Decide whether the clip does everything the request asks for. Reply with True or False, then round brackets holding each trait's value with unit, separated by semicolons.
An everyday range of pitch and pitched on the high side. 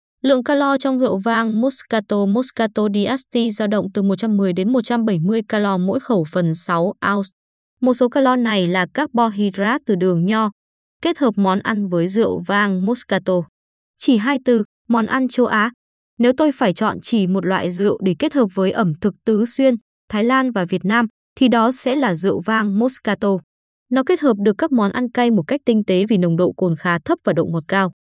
True (4.5 semitones; 220 Hz)